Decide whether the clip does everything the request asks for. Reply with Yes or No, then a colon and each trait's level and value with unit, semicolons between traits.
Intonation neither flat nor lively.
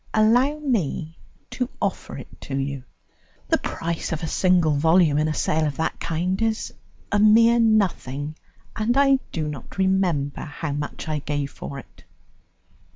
No: wide, 6.6 semitones